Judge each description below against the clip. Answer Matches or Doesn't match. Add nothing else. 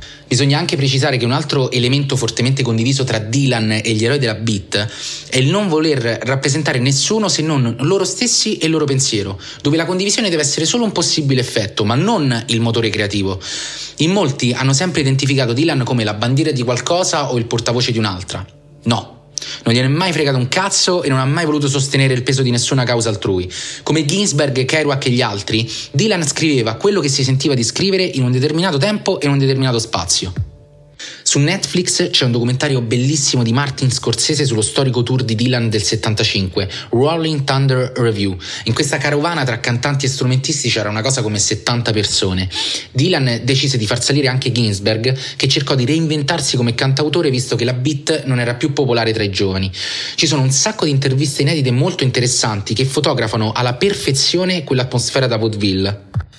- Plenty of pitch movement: Doesn't match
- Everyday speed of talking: Doesn't match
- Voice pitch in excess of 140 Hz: Doesn't match